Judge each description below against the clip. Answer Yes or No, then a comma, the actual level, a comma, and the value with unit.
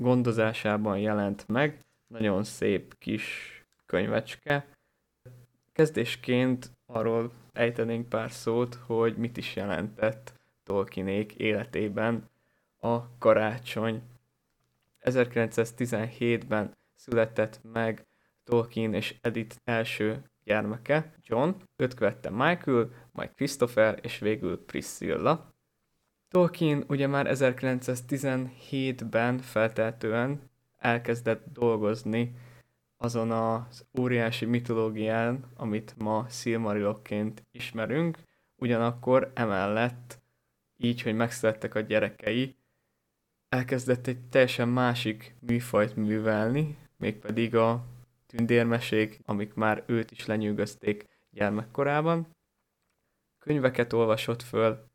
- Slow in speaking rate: Yes, slow, 85 wpm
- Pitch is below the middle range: Yes, low, 115 Hz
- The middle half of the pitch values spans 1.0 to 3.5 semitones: Yes, narrow, 2.4 semitones